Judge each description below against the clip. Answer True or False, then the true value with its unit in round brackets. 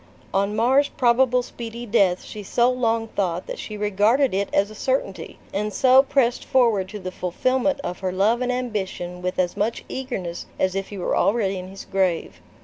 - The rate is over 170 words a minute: True (190 wpm)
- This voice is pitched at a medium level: False (210 Hz)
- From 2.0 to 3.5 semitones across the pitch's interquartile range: False (4.4 semitones)